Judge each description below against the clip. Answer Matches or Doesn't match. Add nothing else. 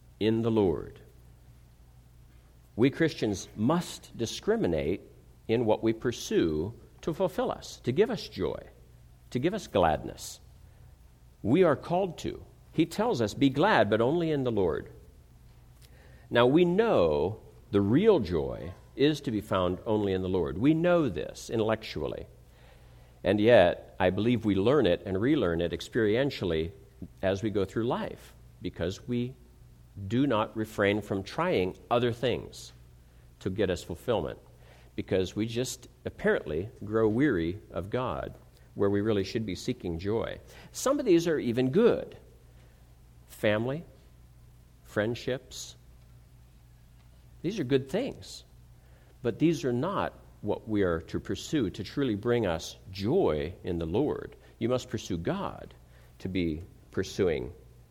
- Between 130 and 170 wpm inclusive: Matches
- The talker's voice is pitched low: Matches